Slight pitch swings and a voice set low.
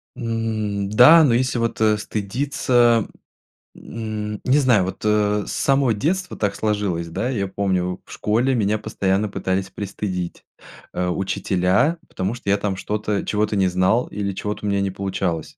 No: average, 3.1 semitones; low, 105 Hz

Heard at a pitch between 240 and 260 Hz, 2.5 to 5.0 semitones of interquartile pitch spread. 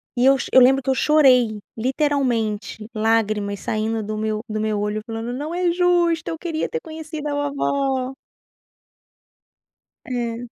No: very high, 255 Hz; wide, 5.5 semitones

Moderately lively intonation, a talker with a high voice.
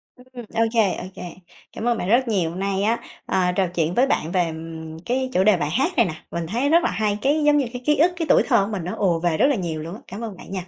No: wide, 5.8 semitones; high, 205 Hz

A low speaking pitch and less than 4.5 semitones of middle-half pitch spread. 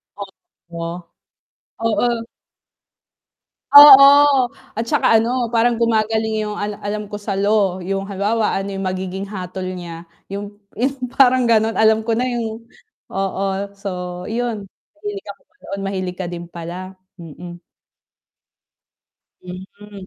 No: high, 205 Hz; average, 3.3 semitones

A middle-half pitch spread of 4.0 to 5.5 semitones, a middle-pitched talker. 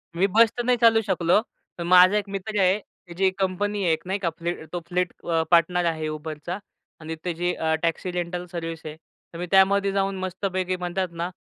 No: narrow, 2.4 semitones; medium, 180 Hz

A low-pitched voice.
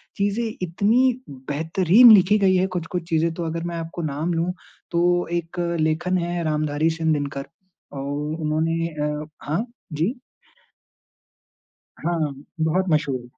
No: medium, 165 Hz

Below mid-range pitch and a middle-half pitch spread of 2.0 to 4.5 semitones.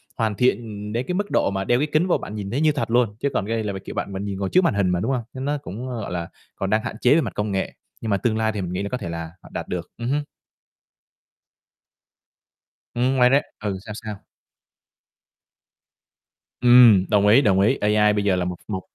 Yes: low, 110 Hz; average, 4.1 semitones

